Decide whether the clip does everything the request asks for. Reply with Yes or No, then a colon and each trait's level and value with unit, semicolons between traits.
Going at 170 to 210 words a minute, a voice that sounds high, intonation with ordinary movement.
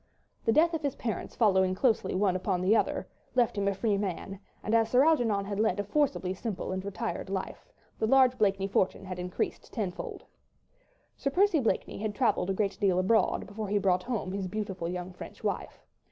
Yes: average, 195 wpm; high, 200 Hz; average, 3.4 semitones